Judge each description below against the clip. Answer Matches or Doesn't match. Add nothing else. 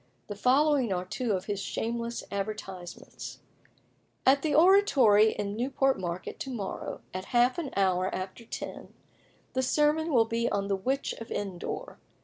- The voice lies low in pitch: Doesn't match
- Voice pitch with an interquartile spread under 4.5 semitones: Doesn't match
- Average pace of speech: Matches